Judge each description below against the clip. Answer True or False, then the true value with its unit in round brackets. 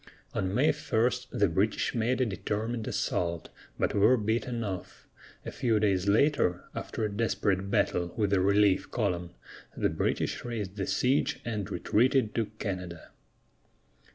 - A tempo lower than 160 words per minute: True (145 wpm)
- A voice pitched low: True (105 Hz)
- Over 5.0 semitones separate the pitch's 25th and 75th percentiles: False (3.5 semitones)